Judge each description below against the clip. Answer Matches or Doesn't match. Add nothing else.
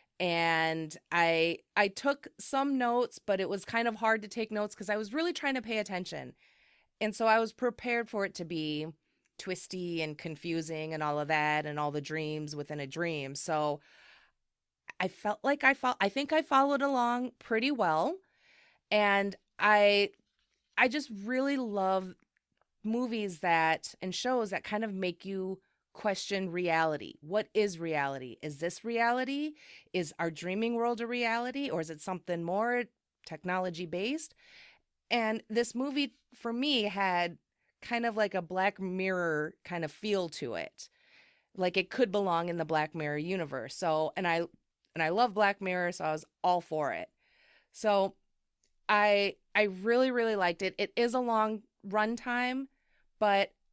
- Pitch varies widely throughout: Matches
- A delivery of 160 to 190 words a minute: Matches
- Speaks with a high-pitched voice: Matches